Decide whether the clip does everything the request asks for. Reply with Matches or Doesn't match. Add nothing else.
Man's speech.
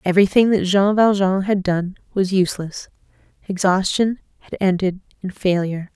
Doesn't match